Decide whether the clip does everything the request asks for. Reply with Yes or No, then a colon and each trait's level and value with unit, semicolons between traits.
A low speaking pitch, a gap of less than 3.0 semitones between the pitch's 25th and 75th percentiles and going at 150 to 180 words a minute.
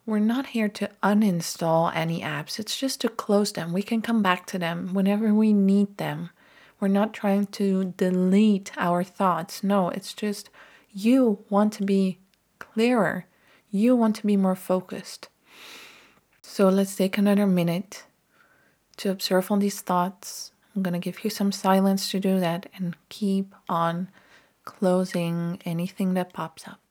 No: high, 195 Hz; narrow, 2.5 semitones; average, 160 wpm